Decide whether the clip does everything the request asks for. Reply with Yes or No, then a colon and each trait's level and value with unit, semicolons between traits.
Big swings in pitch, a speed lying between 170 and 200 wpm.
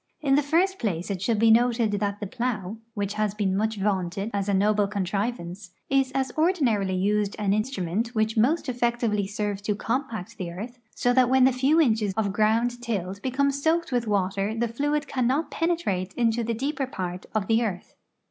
No: average, 4.2 semitones; average, 190 wpm